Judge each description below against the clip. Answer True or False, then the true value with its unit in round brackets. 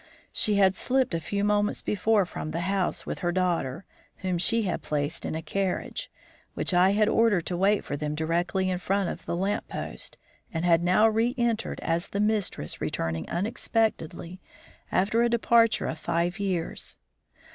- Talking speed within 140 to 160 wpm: False (170 wpm)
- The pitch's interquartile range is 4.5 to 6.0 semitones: False (3.7 semitones)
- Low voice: False (190 Hz)